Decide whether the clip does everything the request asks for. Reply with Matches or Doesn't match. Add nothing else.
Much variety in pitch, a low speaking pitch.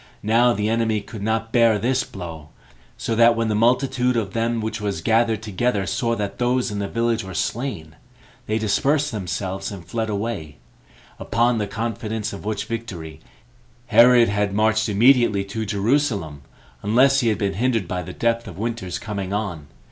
Doesn't match